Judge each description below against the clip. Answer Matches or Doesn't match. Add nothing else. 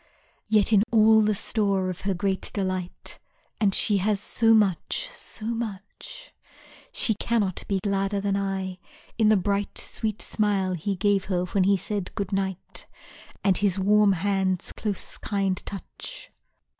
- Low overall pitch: Doesn't match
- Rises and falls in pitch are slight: Matches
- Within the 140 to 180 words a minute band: Matches